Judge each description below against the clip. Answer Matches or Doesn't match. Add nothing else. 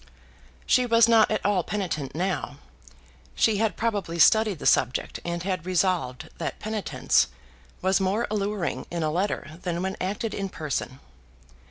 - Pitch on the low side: Doesn't match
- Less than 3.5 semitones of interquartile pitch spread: Doesn't match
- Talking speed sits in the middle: Matches